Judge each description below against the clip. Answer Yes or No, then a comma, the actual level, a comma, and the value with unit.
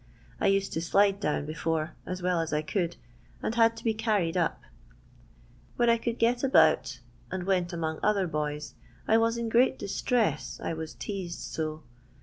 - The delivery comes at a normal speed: Yes, average, 175 wpm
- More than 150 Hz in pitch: Yes, medium, 185 Hz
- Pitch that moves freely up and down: Yes, wide, 5.9 semitones